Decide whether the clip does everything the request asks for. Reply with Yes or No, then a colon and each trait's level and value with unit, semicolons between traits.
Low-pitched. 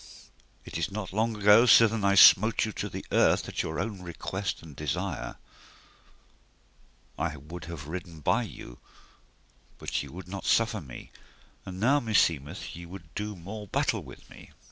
Yes: very low, 95 Hz